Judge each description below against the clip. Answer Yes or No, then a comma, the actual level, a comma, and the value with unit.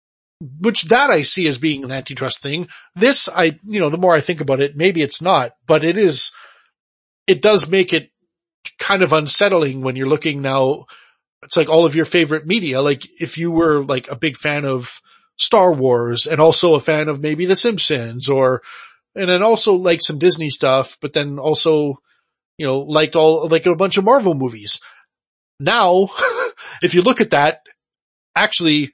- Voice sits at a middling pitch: Yes, medium, 160 Hz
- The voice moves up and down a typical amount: Yes, average, 4.2 semitones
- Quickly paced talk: No, average, 185 wpm